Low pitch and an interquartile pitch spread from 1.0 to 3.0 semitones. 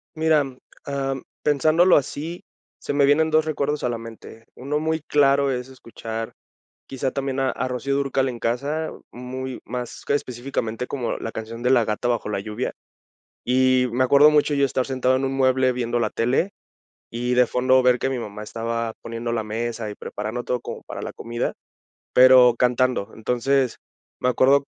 Yes: low, 130 Hz; average, 2.7 semitones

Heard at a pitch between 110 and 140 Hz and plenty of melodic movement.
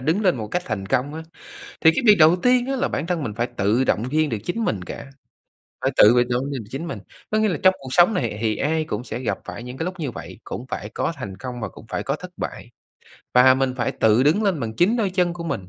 Yes: low, 135 Hz; wide, 6.8 semitones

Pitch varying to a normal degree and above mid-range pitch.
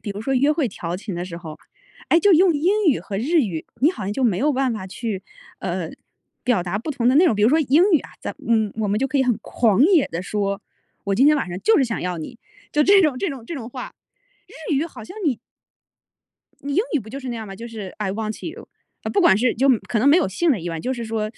No: wide, 6.2 semitones; high, 240 Hz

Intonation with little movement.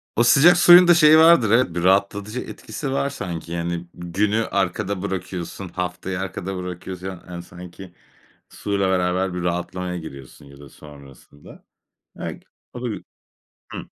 No: average, 3.3 semitones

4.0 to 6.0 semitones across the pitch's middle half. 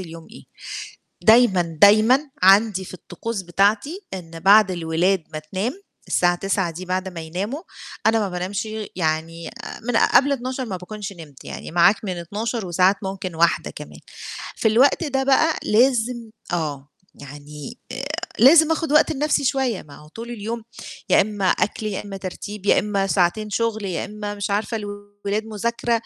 Yes: average, 4.3 semitones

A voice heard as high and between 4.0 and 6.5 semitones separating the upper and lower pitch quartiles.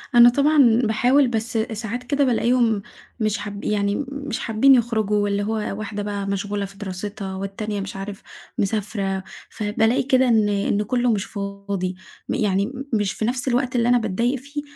No: high, 215 Hz; average, 3.2 semitones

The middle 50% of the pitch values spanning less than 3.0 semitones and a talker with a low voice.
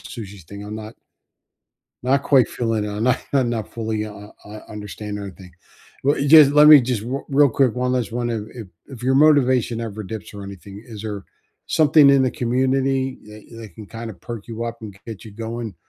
No: average, 3.8 semitones; low, 115 Hz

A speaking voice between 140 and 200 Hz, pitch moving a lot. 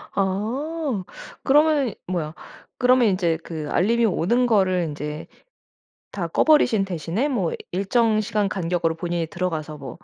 Yes: high, 190 Hz; wide, 6.0 semitones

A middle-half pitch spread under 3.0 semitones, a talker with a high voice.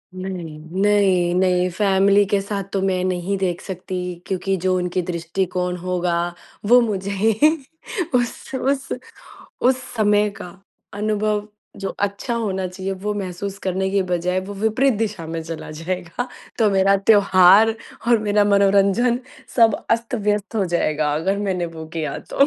Yes: narrow, 2.4 semitones; high, 195 Hz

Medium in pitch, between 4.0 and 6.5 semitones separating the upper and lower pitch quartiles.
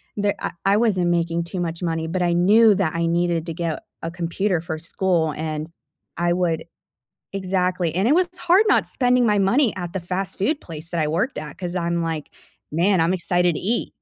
No: medium, 175 Hz; average, 2.8 semitones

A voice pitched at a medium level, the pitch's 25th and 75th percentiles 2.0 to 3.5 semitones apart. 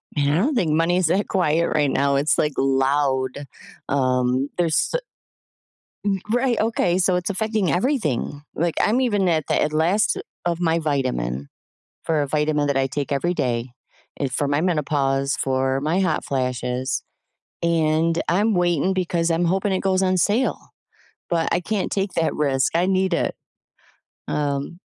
No: medium, 160 Hz; average, 4.9 semitones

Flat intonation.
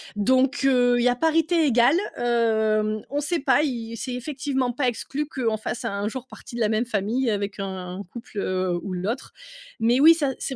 No: average, 3.8 semitones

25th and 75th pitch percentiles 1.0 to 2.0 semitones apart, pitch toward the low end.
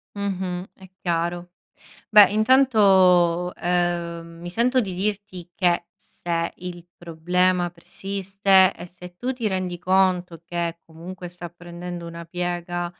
No: narrow, 1.7 semitones; medium, 180 Hz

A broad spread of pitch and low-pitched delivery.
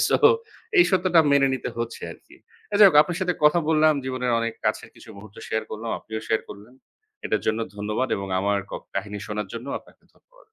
Yes: wide, 6.2 semitones; low, 115 Hz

